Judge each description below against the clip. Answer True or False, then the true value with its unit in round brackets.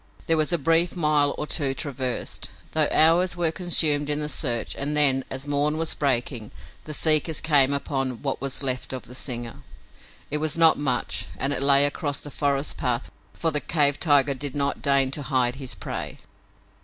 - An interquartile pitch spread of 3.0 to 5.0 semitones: False (2.4 semitones)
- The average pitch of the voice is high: False (145 Hz)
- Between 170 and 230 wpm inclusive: True (190 wpm)